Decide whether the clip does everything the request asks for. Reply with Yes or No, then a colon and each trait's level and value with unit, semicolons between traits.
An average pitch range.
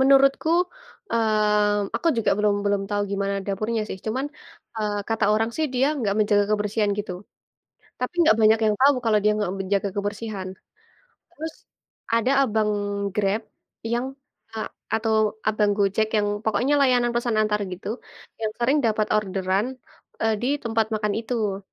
No: narrow, 2.1 semitones